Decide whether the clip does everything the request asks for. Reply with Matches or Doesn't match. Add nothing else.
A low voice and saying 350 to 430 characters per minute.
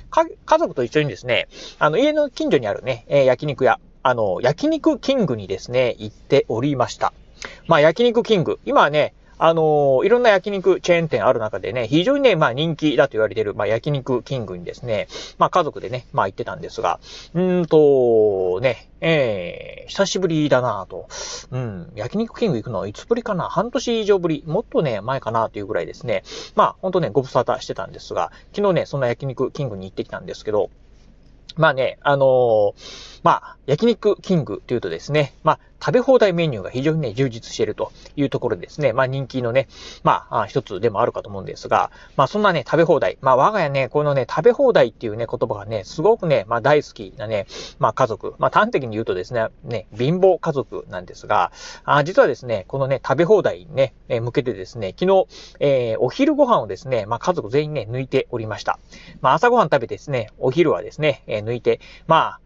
Doesn't match